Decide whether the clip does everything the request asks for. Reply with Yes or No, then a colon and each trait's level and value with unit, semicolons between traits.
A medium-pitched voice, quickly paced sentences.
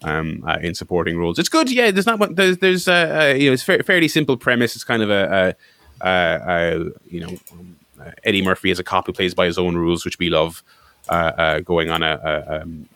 No: very low, 90 Hz; fast, 250 wpm